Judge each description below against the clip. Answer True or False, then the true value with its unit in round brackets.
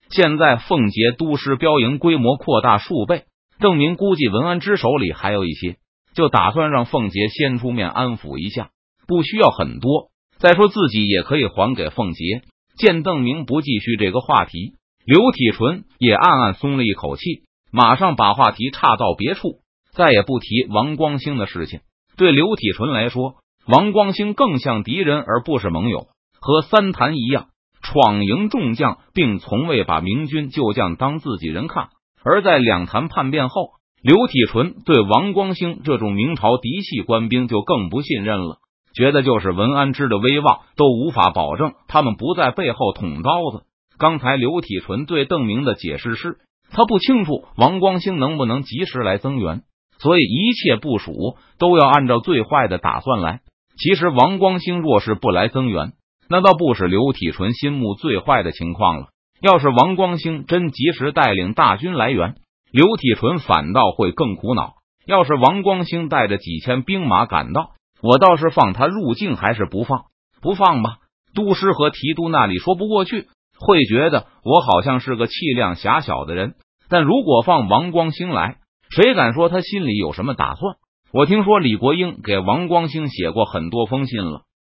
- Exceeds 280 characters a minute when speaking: False (260 characters per minute)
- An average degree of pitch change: False (7.3 semitones)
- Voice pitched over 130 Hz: True (140 Hz)